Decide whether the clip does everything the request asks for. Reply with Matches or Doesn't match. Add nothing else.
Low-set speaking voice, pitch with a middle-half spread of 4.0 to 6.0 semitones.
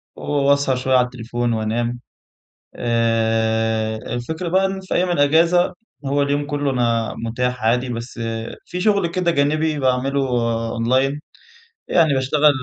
Matches